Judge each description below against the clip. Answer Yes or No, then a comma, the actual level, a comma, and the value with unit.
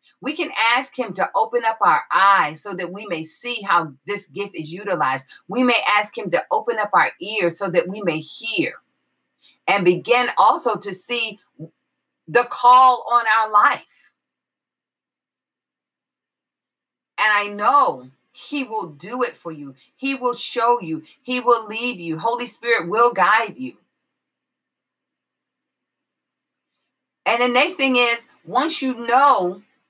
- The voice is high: Yes, high, 230 Hz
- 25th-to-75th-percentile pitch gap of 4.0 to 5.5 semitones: Yes, average, 4.6 semitones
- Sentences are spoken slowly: No, average, 145 wpm